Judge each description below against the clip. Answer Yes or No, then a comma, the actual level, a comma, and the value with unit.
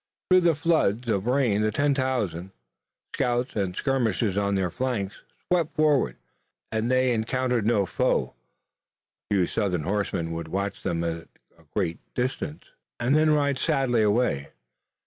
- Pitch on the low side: Yes, low, 115 Hz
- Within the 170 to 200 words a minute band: No, average, 145 wpm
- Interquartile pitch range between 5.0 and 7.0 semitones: Yes, average, 5.3 semitones